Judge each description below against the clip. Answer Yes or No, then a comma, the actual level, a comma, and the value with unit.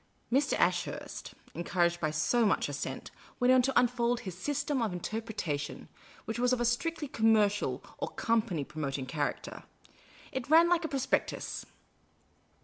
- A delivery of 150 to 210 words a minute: No, average, 140 wpm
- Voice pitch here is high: Yes, high, 230 Hz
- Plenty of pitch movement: Yes, wide, 6.9 semitones